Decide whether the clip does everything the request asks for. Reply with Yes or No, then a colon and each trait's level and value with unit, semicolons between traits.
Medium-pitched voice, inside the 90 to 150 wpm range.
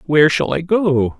No: medium, 145 Hz; average, 200 wpm